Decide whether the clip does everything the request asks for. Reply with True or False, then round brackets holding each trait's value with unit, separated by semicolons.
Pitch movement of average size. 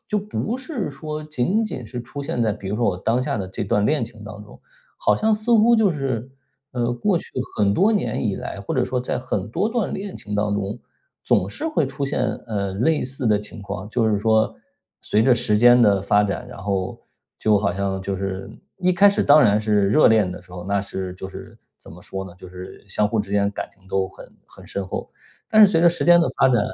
False (7.3 semitones)